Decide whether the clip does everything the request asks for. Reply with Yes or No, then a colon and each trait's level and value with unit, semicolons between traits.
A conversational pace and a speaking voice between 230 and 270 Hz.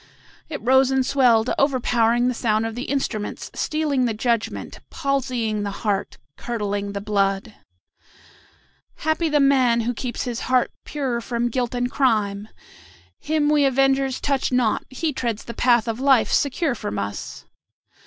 Yes: average, 150 wpm; high, 245 Hz